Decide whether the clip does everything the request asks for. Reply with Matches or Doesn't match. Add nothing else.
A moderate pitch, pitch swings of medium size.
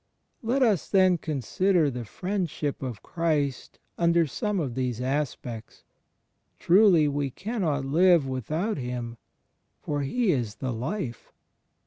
Doesn't match